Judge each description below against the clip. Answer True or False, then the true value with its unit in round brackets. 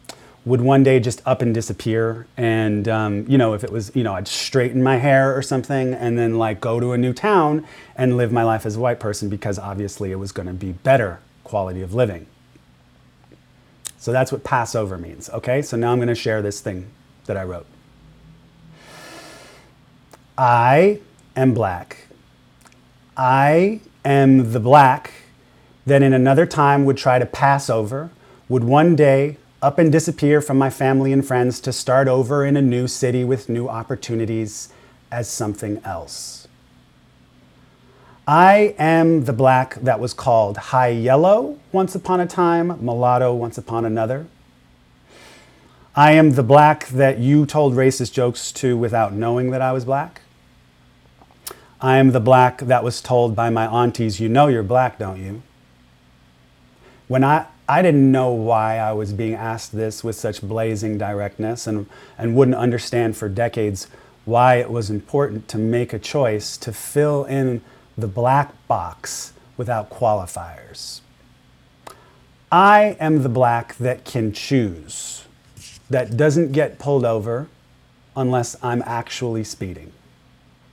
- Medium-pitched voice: False (125 Hz)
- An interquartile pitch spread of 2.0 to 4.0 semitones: True (3.6 semitones)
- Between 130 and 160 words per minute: True (155 wpm)